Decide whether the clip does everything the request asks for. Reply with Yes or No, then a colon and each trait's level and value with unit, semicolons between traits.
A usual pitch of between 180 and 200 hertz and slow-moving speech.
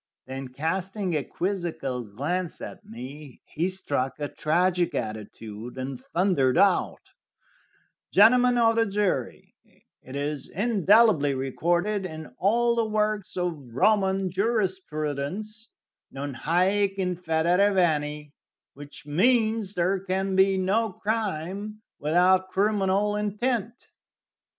Yes: medium, 185 Hz; slow, 110 wpm